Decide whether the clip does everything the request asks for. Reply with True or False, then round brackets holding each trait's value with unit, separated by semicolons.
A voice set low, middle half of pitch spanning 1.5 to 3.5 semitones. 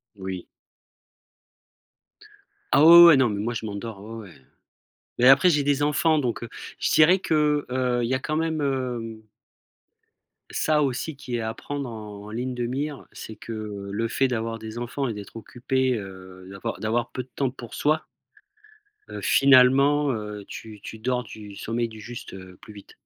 False (120 Hz; 4.1 semitones)